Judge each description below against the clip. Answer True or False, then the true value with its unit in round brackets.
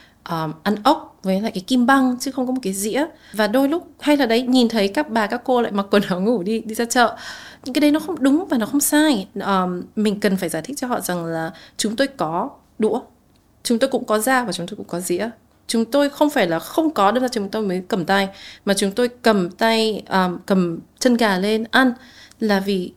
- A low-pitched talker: False (225 Hz)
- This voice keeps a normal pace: False (255 wpm)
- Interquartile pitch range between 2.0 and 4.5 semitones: False (5.0 semitones)